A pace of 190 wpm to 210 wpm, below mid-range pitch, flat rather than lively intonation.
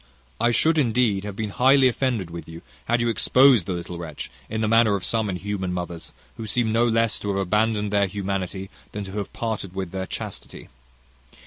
No: average, 200 wpm; low, 105 Hz; average, 3.4 semitones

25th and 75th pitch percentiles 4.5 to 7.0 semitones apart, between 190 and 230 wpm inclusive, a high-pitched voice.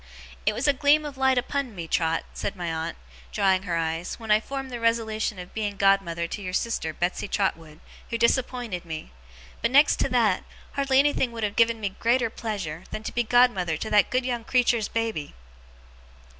Yes: average, 5.3 semitones; average, 195 wpm; high, 220 Hz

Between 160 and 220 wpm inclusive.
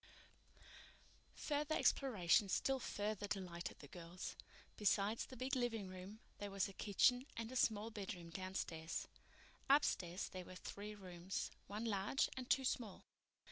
No: slow, 135 wpm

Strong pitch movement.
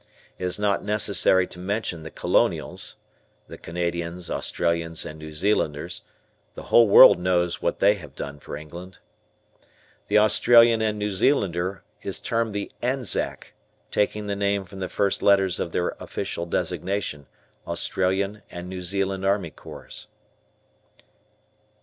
No: average, 3.0 semitones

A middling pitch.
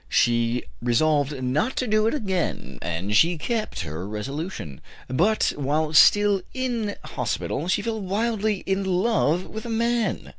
Yes: medium, 180 Hz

